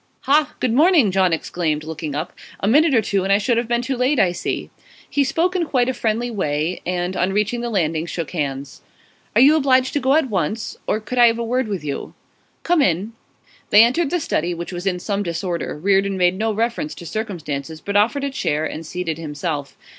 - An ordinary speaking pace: No, fast, 220 wpm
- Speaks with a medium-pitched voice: No, high, 200 Hz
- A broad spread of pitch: Yes, wide, 6.6 semitones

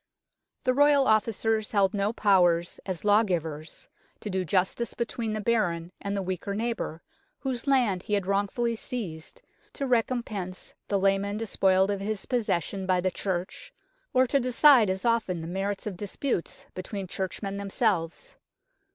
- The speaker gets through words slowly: No, average, 155 wpm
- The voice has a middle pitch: No, high, 200 Hz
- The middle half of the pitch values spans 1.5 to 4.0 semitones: Yes, average, 3.7 semitones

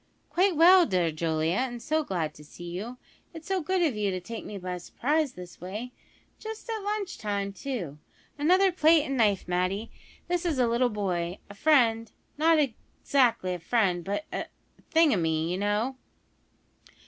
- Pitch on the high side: Yes, high, 230 Hz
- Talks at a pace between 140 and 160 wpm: No, average, 175 wpm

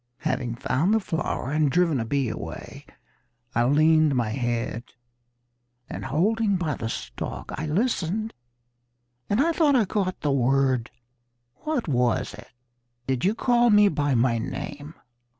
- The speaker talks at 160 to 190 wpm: No, average, 145 wpm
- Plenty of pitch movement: Yes, wide, 8.1 semitones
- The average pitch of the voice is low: No, medium, 150 Hz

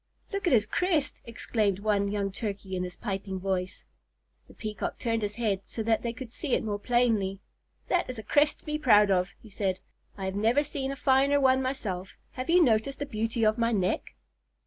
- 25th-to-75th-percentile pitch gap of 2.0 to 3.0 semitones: No, average, 4.7 semitones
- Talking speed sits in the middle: No, fast, 210 wpm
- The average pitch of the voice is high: Yes, high, 220 Hz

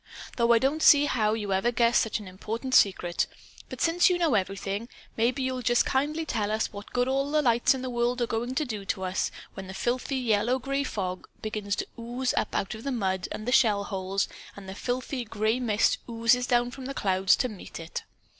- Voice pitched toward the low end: No, high, 235 Hz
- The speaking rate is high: Yes, fast, 220 wpm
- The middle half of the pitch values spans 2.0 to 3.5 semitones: No, average, 4.0 semitones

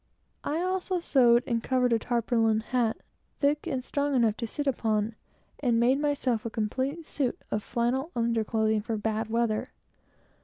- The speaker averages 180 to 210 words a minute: No, average, 165 wpm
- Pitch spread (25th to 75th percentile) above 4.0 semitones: No, average, 3.5 semitones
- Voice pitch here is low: No, high, 235 Hz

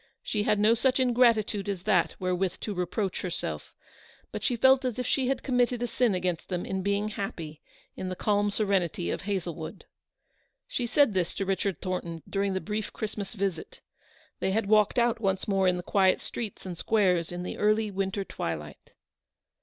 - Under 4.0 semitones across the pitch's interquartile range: Yes, average, 3.1 semitones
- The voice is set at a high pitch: Yes, high, 200 Hz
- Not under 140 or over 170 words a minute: No, average, 185 wpm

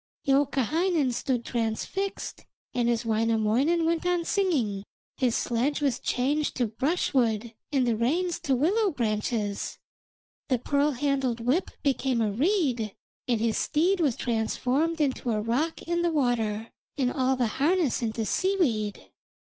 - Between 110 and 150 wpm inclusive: Yes, average, 140 wpm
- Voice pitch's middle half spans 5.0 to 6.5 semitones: Yes, wide, 5.4 semitones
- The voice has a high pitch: Yes, very high, 260 Hz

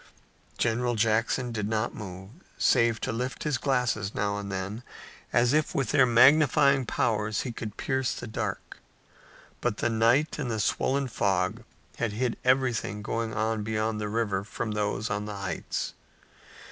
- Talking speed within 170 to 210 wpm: No, average, 160 wpm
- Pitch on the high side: No, low, 115 Hz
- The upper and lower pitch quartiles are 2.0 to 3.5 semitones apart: Yes, average, 3.0 semitones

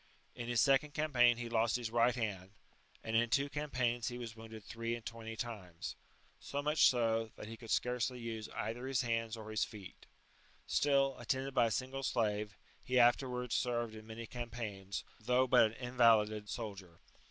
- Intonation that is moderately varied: No, narrow, 2.0 semitones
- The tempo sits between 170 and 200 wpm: Yes, average, 175 wpm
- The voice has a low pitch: Yes, low, 115 Hz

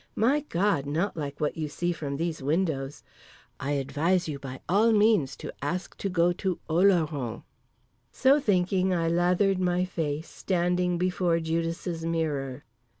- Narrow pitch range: No, average, 3.6 semitones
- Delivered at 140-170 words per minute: Yes, average, 145 wpm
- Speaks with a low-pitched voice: No, medium, 170 Hz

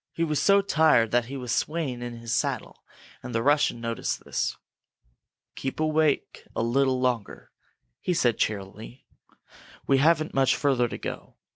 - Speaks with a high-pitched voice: No, low, 130 Hz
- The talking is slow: No, average, 160 wpm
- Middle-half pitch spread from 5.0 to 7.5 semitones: No, average, 4.4 semitones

